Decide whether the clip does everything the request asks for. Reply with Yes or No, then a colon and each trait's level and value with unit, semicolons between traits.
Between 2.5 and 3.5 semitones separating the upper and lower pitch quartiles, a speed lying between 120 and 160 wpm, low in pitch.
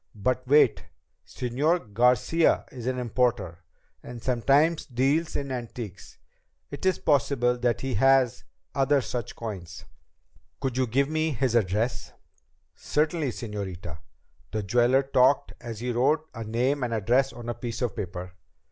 Yes: average, 3.1 semitones; average, 140 wpm; low, 125 Hz